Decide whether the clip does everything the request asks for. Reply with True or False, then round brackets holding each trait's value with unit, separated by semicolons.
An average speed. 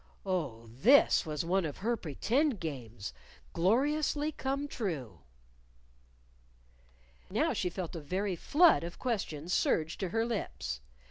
False (125 wpm)